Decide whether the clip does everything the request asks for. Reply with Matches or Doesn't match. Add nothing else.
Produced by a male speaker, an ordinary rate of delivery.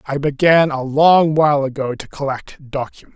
Matches